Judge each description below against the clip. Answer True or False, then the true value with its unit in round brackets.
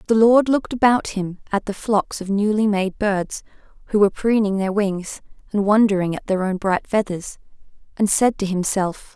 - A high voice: True (205 Hz)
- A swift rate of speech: False (185 wpm)